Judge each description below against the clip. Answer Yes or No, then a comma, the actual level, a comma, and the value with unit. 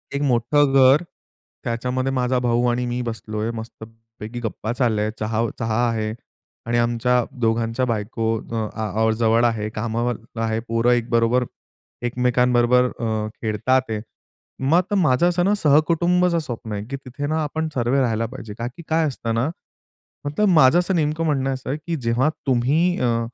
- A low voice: Yes, low, 120 Hz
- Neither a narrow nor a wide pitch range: Yes, average, 3.2 semitones